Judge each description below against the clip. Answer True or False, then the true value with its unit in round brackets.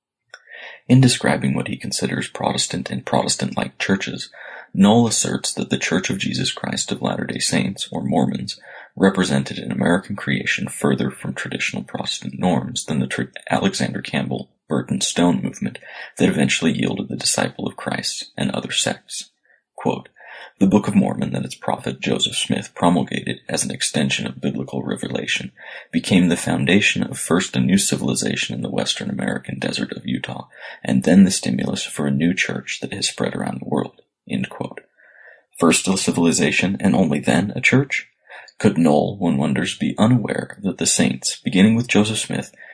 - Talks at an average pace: True (165 wpm)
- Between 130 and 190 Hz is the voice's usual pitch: False (95 Hz)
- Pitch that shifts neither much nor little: False (8.5 semitones)